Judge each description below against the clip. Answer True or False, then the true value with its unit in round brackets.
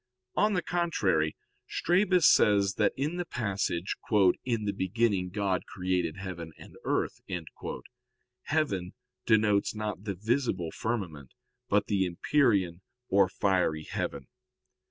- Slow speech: True (115 wpm)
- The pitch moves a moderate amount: True (4.4 semitones)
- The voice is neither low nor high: False (100 Hz)